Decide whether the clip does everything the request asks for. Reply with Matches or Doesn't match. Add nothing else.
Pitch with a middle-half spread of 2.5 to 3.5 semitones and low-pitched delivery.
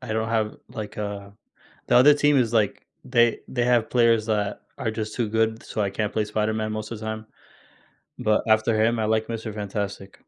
Doesn't match